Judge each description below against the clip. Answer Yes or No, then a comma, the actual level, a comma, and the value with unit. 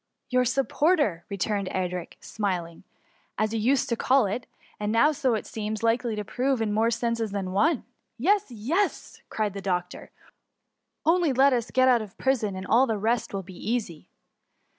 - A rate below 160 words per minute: No, average, 195 wpm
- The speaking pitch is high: Yes, high, 225 Hz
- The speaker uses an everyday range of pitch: Yes, average, 4.3 semitones